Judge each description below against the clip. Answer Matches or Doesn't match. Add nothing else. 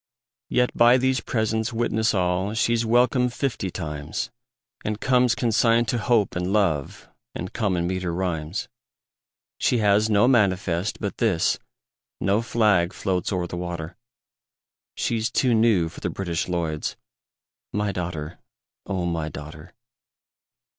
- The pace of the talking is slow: Matches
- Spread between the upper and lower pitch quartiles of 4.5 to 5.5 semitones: Matches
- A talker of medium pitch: Doesn't match